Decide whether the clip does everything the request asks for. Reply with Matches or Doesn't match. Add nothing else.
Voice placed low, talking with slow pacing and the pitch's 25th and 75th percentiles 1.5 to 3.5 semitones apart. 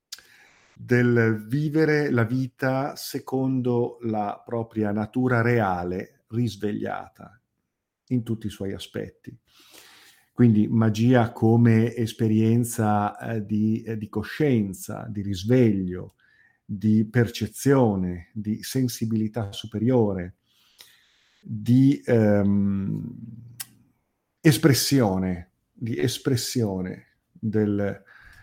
Matches